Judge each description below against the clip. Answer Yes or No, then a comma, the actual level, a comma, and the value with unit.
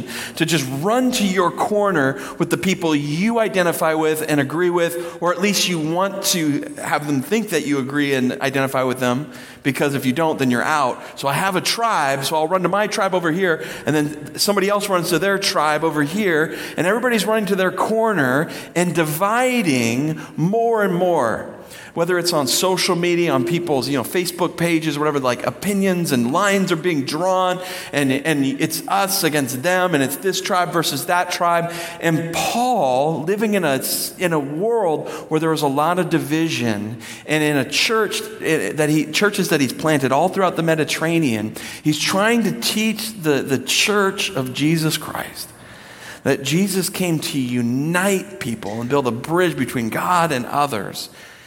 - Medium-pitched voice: Yes, medium, 165 Hz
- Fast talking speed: No, average, 185 wpm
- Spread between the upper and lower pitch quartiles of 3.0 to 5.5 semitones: Yes, average, 4.5 semitones